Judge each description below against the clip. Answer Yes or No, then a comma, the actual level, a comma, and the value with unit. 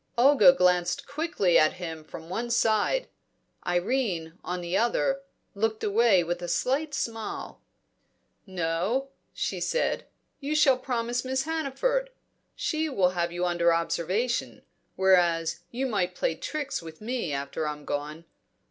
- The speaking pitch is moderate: No, high, 200 Hz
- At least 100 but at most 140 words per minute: Yes, slow, 135 wpm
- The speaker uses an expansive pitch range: Yes, wide, 7.3 semitones